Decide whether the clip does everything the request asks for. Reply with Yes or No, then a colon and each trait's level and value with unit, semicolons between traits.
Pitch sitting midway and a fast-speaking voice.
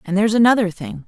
No: high, 205 Hz; fast, 225 wpm